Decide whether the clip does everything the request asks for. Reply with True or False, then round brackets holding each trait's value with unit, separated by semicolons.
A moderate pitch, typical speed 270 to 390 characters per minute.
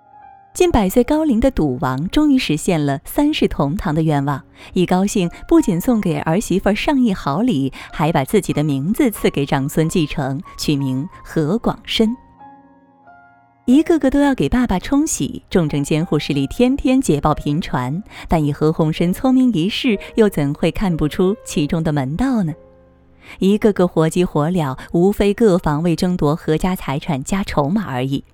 False (175 Hz; 250 characters per minute)